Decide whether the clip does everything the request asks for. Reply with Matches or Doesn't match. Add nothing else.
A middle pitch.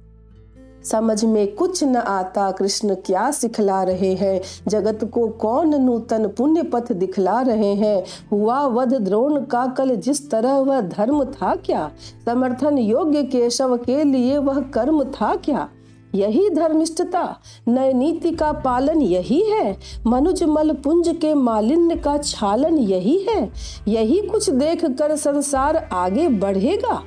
Doesn't match